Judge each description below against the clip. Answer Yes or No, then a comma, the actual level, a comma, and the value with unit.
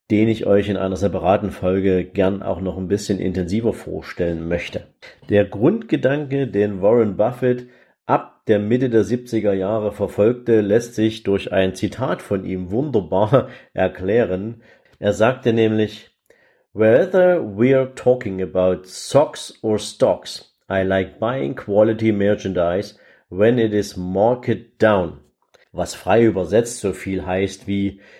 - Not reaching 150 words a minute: Yes, average, 135 wpm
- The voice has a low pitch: Yes, low, 105 Hz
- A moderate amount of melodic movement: Yes, average, 3.0 semitones